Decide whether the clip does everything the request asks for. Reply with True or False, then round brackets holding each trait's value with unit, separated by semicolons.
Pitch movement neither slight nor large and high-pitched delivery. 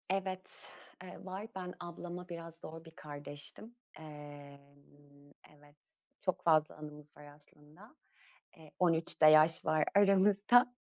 False (3.9 semitones; 160 Hz)